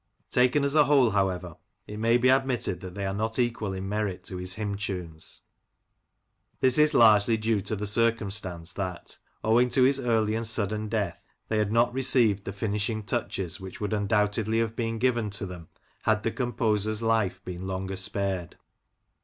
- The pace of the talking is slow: No, average, 180 wpm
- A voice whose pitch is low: Yes, low, 105 Hz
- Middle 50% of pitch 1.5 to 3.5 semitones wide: Yes, average, 3.1 semitones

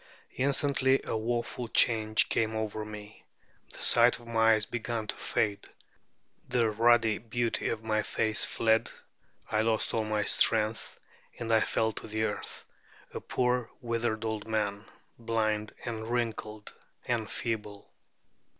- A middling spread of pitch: No, narrow, 1.5 semitones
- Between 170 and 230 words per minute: No, average, 140 wpm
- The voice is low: Yes, low, 110 Hz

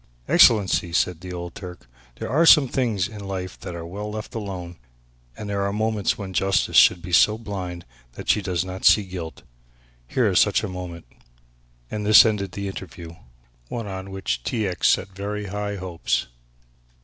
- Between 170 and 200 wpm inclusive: Yes, average, 185 wpm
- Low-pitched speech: Yes, very low, 95 Hz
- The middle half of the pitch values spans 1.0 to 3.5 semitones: Yes, narrow, 2.6 semitones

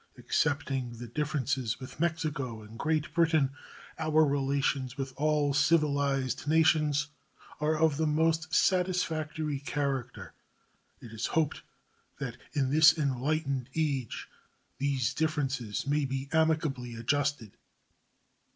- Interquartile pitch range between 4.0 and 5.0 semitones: No, average, 2.9 semitones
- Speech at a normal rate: No, slow, 110 wpm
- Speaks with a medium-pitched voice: Yes, medium, 145 Hz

